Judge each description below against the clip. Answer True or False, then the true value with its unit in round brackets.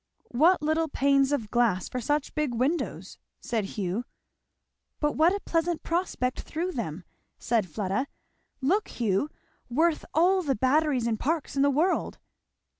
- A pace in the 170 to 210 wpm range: False (145 wpm)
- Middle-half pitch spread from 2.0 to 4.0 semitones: False (5.5 semitones)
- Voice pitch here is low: False (280 Hz)